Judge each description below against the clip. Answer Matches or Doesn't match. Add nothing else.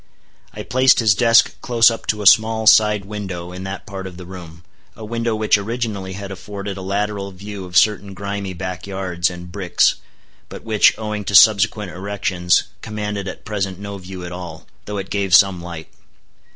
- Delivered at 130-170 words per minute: Doesn't match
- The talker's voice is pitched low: Matches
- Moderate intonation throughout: Doesn't match